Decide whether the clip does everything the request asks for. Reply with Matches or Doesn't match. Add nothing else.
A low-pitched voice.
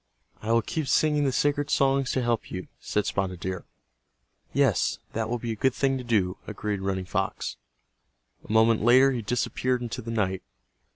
Matches